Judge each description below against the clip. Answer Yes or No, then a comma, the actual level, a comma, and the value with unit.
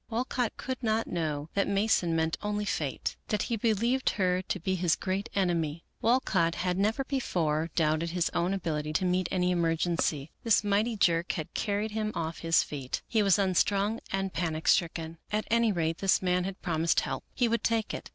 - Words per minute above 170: Yes, average, 190 wpm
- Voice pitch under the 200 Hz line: Yes, medium, 185 Hz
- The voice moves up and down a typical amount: Yes, average, 4.2 semitones